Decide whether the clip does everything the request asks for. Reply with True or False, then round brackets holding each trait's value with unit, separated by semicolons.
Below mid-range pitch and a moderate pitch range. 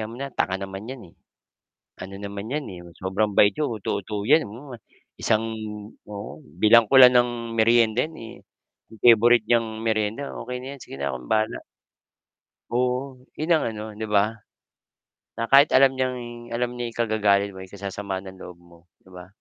True (110 Hz; 3.4 semitones)